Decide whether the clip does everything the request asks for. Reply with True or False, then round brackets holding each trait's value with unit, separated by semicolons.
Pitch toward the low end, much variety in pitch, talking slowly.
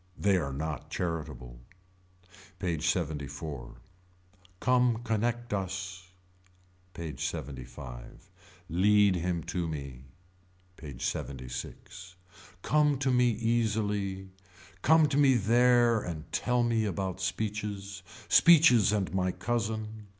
True (95 Hz; 6.2 semitones; 100 wpm)